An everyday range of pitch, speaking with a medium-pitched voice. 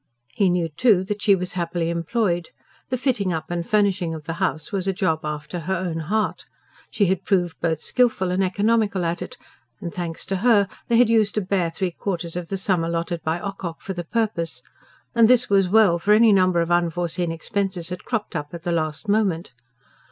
Yes: average, 3.3 semitones; medium, 180 Hz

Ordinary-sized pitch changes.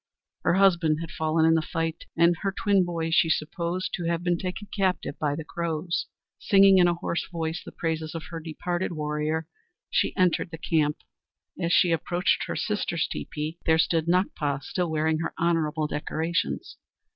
No: narrow, 1.8 semitones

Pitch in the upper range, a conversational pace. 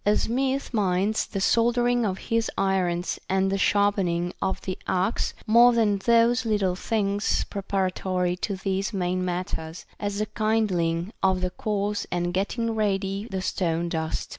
Yes: high, 195 Hz; average, 155 wpm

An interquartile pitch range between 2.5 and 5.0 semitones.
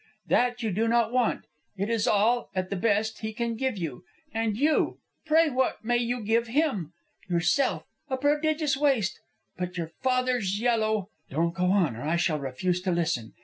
No: wide, 5.4 semitones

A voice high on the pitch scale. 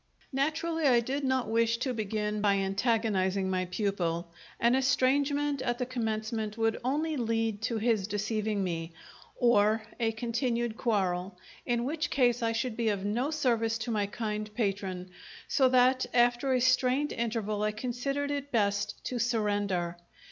Yes: high, 230 Hz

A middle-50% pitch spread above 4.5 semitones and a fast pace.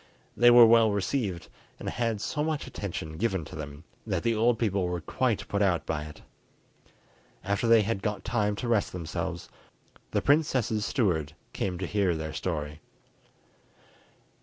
No: average, 5.1 semitones; average, 160 wpm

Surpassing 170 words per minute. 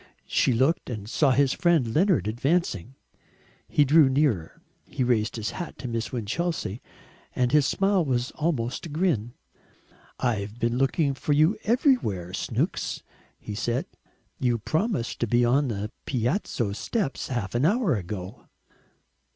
No: average, 145 wpm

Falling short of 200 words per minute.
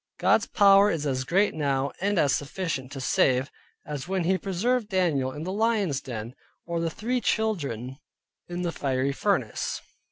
Yes: average, 165 wpm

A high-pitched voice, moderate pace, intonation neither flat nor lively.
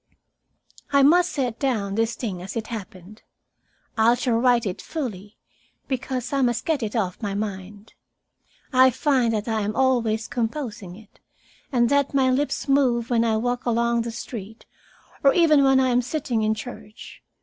Yes: high, 235 Hz; average, 170 wpm; average, 3.3 semitones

